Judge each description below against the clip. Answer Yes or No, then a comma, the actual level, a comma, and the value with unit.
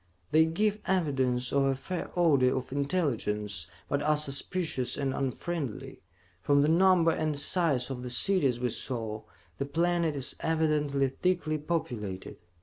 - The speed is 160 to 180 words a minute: No, average, 145 wpm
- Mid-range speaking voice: Yes, medium, 145 Hz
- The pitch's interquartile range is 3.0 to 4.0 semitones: No, average, 4.4 semitones